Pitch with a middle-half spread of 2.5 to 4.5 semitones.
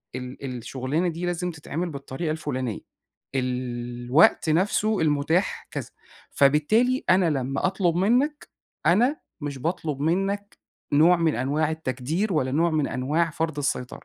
No: average, 4.9 semitones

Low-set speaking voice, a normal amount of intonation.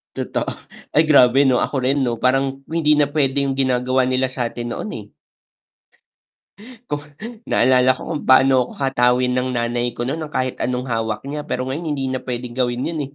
No: low, 130 Hz; narrow, 2.0 semitones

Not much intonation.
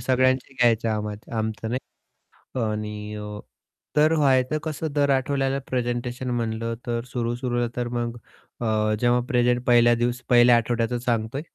Yes: narrow, 1.9 semitones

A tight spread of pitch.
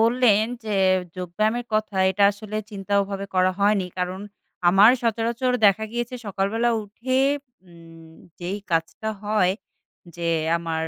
No: average, 3.3 semitones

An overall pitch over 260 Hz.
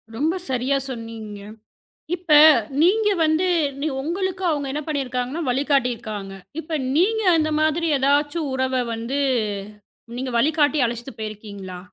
Yes: very high, 275 Hz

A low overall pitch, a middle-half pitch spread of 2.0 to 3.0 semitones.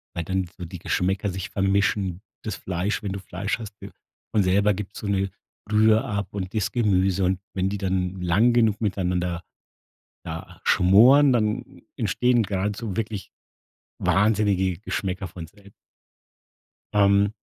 Yes: low, 100 Hz; narrow, 2.4 semitones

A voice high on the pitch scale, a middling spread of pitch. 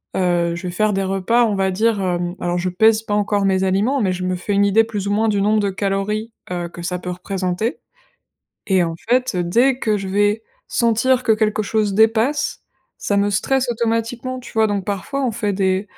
Yes: high, 205 Hz; average, 3.0 semitones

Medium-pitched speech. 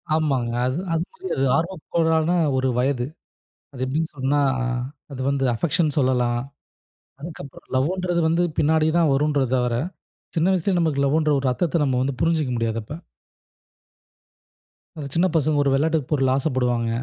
Yes: medium, 145 Hz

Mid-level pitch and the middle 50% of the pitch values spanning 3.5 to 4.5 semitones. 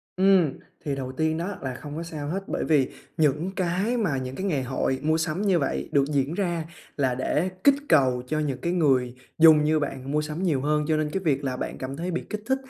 Yes: medium, 155 Hz; average, 4.1 semitones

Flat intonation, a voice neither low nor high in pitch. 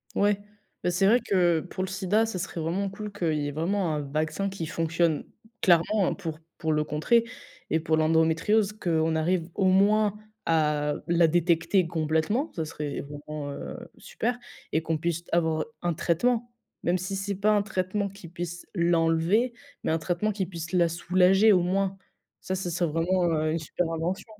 No: average, 3.3 semitones; medium, 175 Hz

